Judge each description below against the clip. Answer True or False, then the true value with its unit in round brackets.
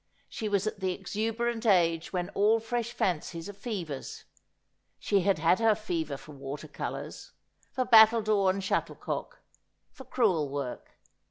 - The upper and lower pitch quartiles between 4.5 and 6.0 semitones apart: True (5.1 semitones)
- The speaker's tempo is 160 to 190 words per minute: False (145 wpm)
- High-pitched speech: True (195 Hz)